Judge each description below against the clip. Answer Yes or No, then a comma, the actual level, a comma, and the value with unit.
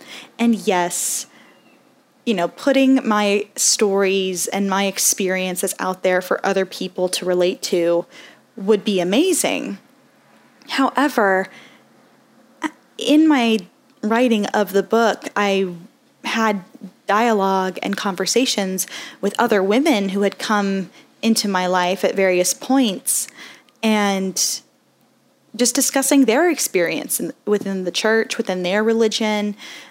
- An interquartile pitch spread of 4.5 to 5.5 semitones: Yes, average, 5.1 semitones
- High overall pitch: Yes, high, 215 Hz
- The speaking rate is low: Yes, slow, 110 wpm